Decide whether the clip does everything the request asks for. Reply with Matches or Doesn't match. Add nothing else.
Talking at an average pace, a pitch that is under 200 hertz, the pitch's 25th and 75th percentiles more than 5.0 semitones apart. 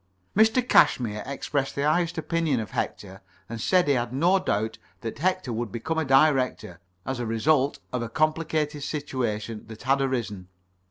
Matches